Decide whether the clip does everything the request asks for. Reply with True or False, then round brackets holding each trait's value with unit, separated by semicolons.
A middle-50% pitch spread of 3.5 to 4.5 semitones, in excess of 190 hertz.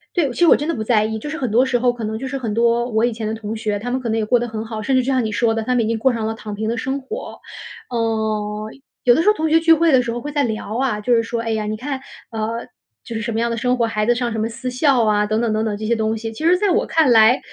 False (2.8 semitones; 230 Hz)